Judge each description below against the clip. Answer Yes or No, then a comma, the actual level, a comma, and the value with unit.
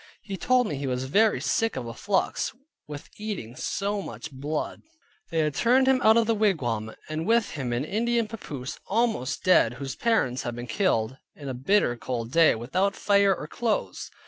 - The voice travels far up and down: Yes, wide, 9.0 semitones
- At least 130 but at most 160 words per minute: No, average, 190 wpm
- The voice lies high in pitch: No, medium, 160 Hz